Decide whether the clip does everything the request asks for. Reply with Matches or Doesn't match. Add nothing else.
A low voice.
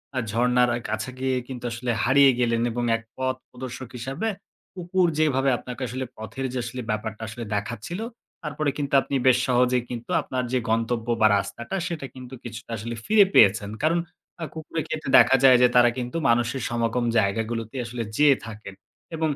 Matches